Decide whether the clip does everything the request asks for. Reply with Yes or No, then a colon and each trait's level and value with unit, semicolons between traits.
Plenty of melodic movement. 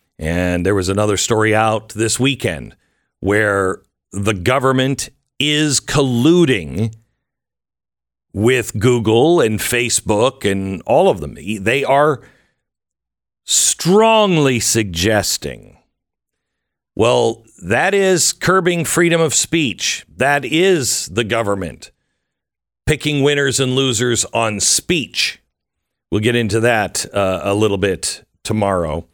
Yes: wide, 5.7 semitones